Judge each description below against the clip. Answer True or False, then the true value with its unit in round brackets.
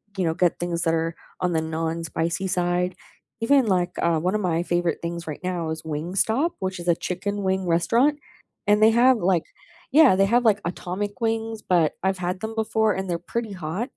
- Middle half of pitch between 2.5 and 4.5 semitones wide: True (4.0 semitones)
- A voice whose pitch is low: False (185 Hz)